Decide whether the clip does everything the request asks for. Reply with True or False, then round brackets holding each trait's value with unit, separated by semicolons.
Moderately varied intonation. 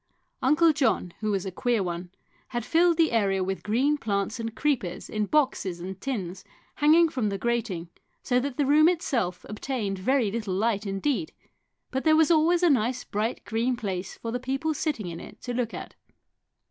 False (6.3 semitones)